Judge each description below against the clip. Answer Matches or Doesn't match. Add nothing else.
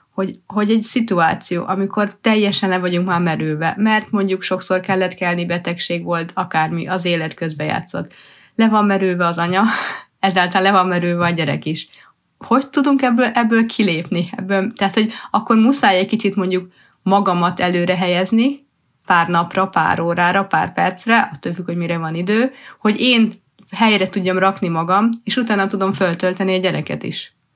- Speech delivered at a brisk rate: Matches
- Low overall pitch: Doesn't match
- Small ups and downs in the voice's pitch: Doesn't match